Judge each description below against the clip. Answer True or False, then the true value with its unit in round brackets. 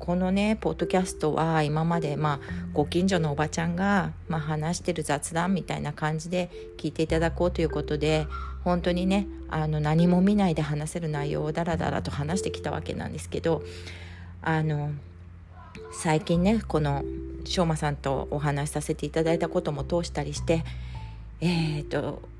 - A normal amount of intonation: True (3.0 semitones)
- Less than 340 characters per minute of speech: False (345 characters per minute)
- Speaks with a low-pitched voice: False (155 Hz)